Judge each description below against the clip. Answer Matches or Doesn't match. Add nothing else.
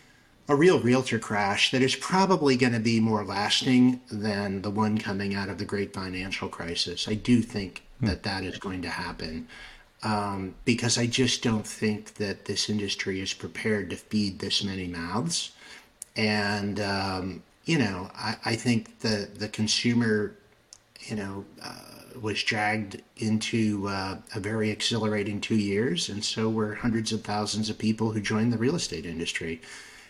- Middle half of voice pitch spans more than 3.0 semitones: Doesn't match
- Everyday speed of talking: Matches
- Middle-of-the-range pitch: Doesn't match